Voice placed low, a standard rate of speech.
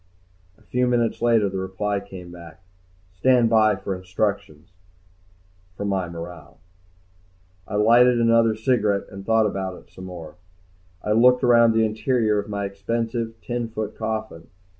Yes: low, 105 Hz; average, 150 wpm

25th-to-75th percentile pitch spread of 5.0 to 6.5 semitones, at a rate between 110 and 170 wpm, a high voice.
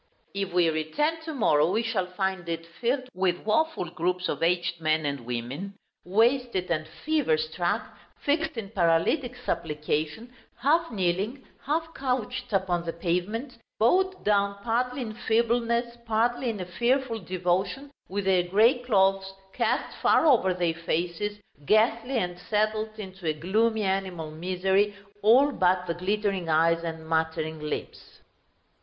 Yes: wide, 5.4 semitones; average, 140 wpm; high, 195 Hz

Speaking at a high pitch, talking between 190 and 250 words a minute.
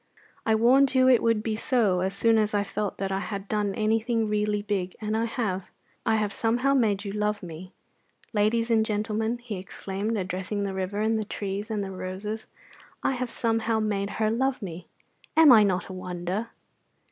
Yes: high, 210 Hz; average, 195 wpm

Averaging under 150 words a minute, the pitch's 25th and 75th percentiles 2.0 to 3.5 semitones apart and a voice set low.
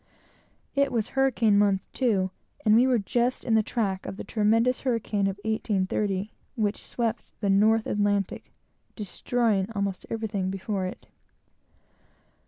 No: slow, 135 wpm; average, 2.7 semitones; high, 215 Hz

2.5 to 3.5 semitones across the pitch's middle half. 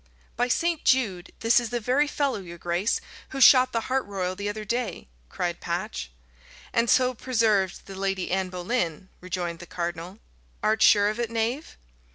No: average, 5.1 semitones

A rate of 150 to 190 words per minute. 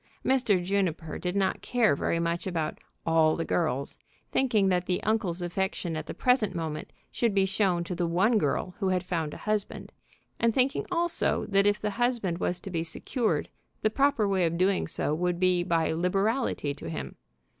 Yes: average, 185 wpm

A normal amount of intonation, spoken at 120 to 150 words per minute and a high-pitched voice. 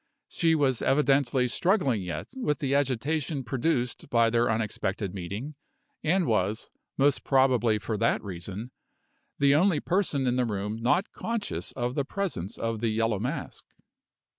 No: average, 4.7 semitones; average, 145 wpm; low, 125 Hz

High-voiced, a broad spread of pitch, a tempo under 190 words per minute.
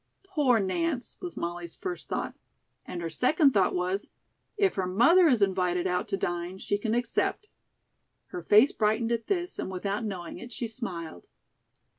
Yes: high, 210 Hz; wide, 6.3 semitones; average, 165 wpm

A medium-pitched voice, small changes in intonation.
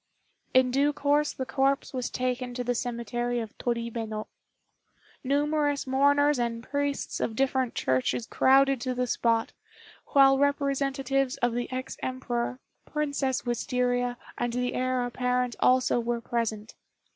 No: very high, 255 Hz; narrow, 2.2 semitones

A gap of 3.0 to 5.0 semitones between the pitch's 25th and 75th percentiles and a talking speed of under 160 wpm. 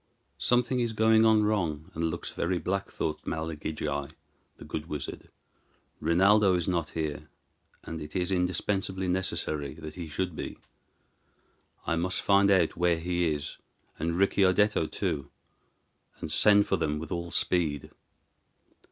Yes: average, 3.7 semitones; average, 140 wpm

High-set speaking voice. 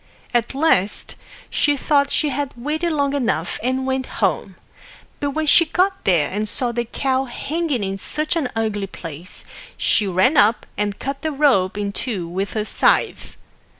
Yes: very high, 250 Hz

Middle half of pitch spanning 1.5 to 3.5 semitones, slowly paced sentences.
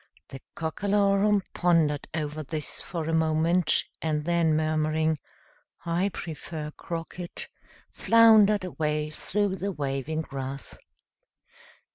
Yes: average, 3.1 semitones; slow, 100 wpm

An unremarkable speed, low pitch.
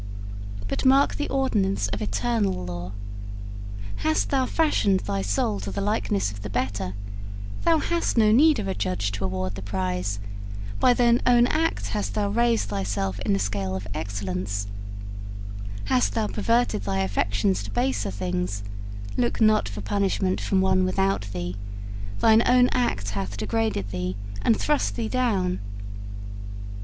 Yes: average, 150 wpm; low, 105 Hz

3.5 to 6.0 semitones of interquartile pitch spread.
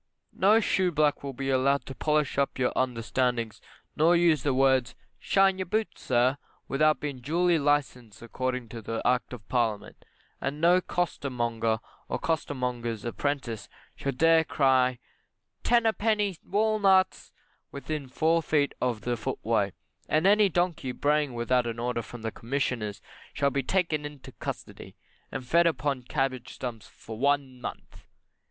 Yes: average, 4.7 semitones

